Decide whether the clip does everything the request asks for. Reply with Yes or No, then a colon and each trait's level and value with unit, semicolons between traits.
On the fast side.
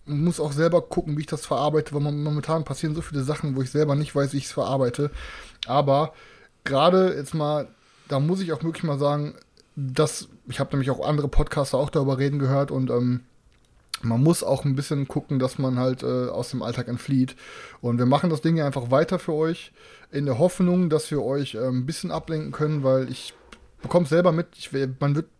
Yes: fast, 215 wpm